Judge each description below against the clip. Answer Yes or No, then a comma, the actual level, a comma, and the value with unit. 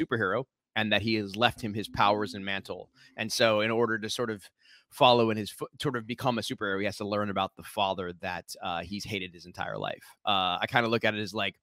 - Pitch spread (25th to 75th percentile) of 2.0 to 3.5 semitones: Yes, average, 2.7 semitones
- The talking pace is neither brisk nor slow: No, fast, 260 wpm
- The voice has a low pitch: Yes, low, 105 Hz